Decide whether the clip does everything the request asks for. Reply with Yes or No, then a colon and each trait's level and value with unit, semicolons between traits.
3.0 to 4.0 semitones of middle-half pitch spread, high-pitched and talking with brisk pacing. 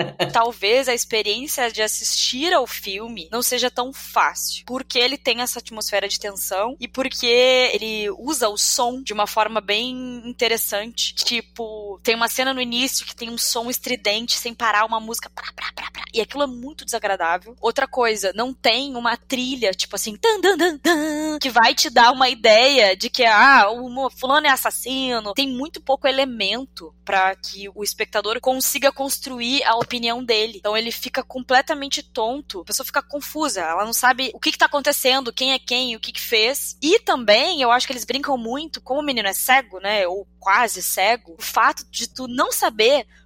Yes: average, 3.4 semitones; high, 245 Hz; fast, 190 wpm